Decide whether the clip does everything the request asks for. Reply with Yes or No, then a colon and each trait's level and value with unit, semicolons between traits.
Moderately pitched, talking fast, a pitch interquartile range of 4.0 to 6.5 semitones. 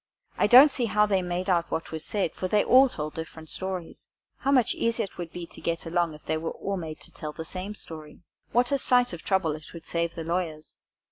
Yes: medium, 175 Hz; fast, 245 wpm; average, 4.3 semitones